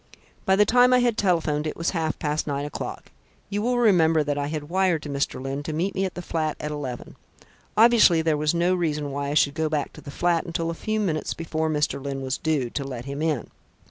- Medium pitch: Yes, medium, 155 Hz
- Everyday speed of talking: No, fast, 240 wpm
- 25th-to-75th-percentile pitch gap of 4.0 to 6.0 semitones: No, average, 3.5 semitones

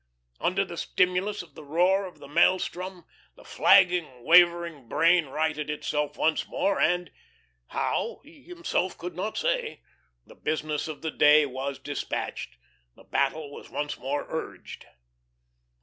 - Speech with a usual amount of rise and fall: Yes, average, 3.7 semitones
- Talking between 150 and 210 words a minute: No, average, 140 wpm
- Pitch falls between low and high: Yes, medium, 170 Hz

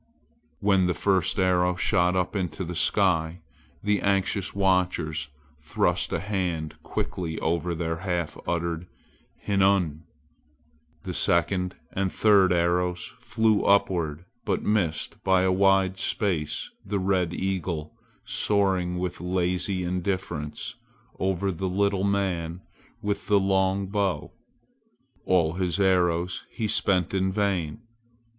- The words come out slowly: Yes, slow, 120 wpm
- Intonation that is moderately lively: No, narrow, 2.0 semitones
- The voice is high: No, very low, 90 Hz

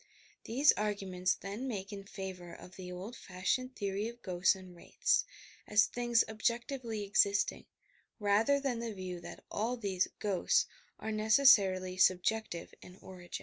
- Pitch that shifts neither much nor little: Yes, average, 3.5 semitones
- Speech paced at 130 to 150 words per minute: Yes, average, 145 wpm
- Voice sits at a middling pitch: No, high, 205 Hz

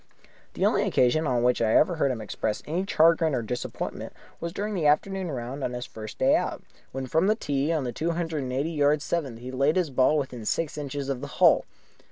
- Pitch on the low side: No, medium, 145 Hz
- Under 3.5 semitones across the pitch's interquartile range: No, average, 4.5 semitones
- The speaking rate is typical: No, fast, 230 wpm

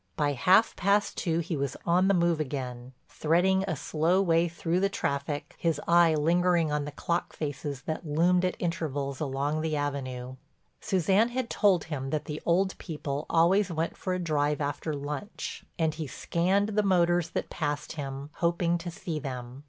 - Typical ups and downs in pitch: Yes, average, 3.5 semitones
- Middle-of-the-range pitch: Yes, medium, 160 Hz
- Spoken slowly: No, average, 175 wpm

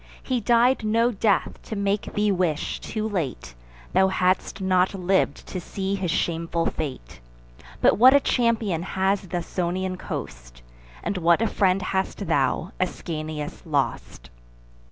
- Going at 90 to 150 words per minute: Yes, average, 140 wpm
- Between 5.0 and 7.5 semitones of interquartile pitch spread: No, average, 3.7 semitones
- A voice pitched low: No, high, 190 Hz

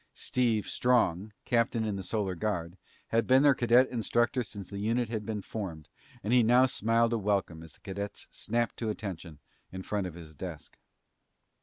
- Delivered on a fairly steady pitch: No, average, 3.8 semitones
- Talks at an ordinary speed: Yes, average, 180 wpm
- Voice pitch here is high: No, low, 105 Hz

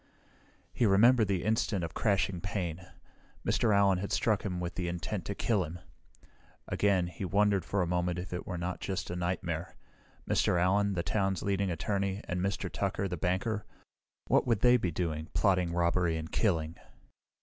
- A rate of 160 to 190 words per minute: Yes, average, 170 wpm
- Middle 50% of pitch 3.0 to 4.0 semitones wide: No, narrow, 2.4 semitones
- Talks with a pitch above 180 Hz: No, very low, 95 Hz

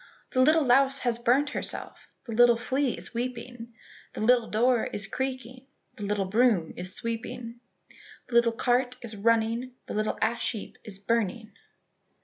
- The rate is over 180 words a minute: No, average, 155 wpm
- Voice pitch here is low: No, high, 235 Hz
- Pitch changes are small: Yes, narrow, 2.2 semitones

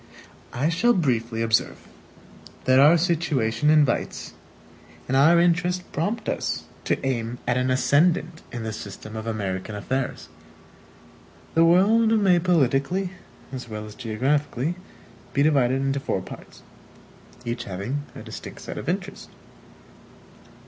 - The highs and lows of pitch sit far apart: Yes, wide, 6.6 semitones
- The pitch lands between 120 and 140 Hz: Yes, low, 135 Hz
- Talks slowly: Yes, slow, 130 wpm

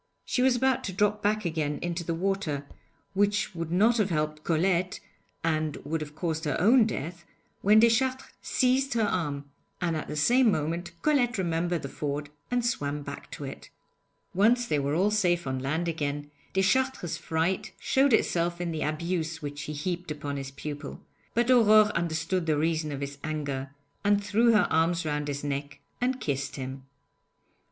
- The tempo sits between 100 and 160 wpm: No, average, 175 wpm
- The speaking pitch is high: No, medium, 170 Hz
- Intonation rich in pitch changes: Yes, wide, 5.8 semitones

